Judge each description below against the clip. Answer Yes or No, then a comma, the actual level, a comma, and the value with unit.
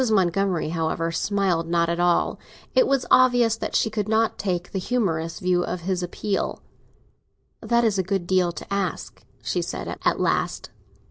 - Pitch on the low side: No, medium, 185 Hz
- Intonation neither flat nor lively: Yes, average, 3.8 semitones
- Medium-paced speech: Yes, average, 170 wpm